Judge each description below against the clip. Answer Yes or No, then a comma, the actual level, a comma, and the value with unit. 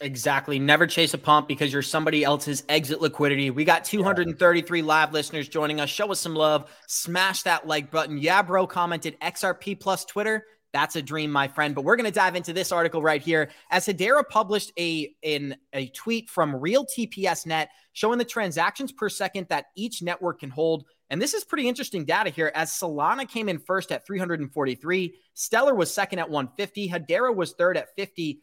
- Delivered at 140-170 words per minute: No, average, 190 wpm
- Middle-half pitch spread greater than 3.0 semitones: Yes, average, 4.5 semitones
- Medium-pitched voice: Yes, medium, 170 Hz